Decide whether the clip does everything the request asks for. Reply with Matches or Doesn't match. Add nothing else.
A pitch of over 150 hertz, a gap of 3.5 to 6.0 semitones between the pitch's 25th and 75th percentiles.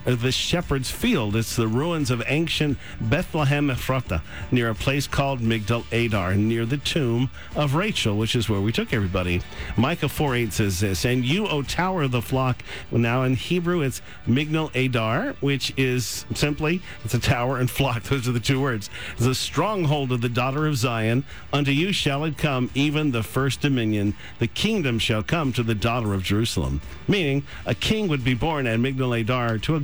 Doesn't match